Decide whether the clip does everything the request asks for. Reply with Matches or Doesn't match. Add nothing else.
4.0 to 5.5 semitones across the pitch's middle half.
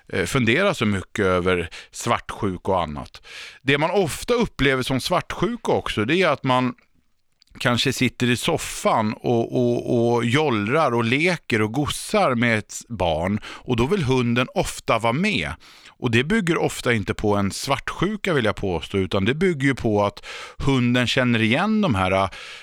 Matches